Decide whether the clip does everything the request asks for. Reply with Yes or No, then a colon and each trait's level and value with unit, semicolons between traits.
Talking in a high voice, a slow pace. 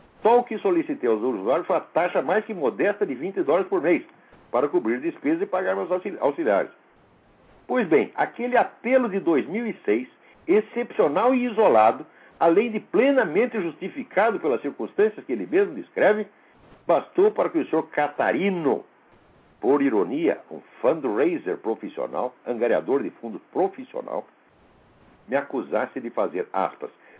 No: very high, 260 Hz; average, 140 wpm